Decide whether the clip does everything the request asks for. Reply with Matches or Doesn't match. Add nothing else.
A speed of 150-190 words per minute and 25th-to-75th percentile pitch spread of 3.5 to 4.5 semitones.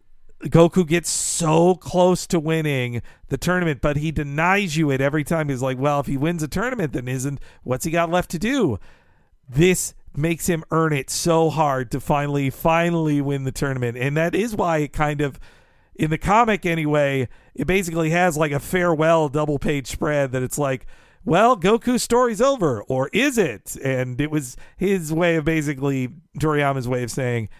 Matches